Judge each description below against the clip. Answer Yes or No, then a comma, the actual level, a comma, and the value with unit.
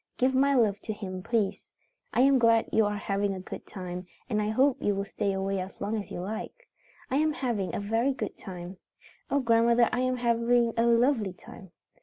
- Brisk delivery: Yes, fast, 210 wpm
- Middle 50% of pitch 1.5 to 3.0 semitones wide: No, average, 3.8 semitones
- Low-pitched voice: No, high, 225 Hz